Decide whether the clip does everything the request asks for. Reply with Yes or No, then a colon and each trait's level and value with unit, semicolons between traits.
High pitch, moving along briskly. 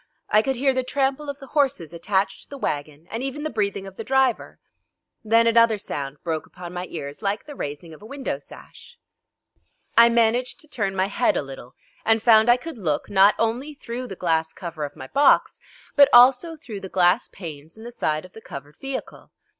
Yes: high, 220 Hz; fast, 210 wpm